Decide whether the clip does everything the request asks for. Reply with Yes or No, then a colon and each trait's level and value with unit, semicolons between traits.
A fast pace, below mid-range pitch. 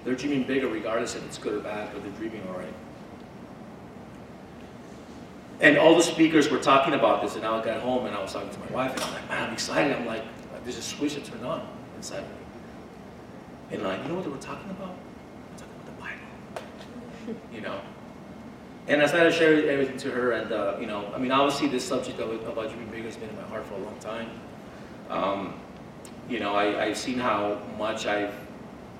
Yes: fast, 220 wpm; low, 125 Hz